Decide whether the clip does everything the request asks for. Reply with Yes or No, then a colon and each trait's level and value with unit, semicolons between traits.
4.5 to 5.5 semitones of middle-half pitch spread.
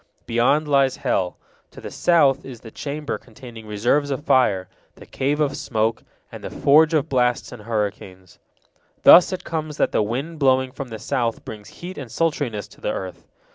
Yes: average, 4.8 semitones